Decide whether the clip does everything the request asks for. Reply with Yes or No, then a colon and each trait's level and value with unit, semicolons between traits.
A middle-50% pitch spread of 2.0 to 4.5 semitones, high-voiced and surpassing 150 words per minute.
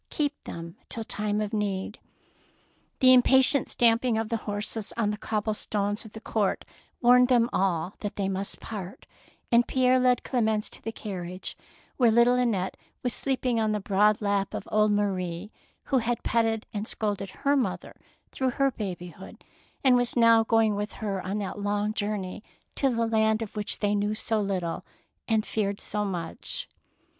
Yes: narrow, 2.6 semitones; high, 215 Hz; average, 170 wpm